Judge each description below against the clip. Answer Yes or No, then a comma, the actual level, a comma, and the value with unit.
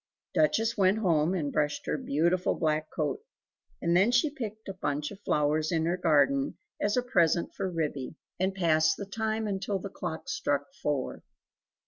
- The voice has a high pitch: No, medium, 175 Hz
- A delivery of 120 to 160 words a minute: No, average, 170 wpm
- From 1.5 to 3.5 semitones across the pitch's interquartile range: No, average, 4.7 semitones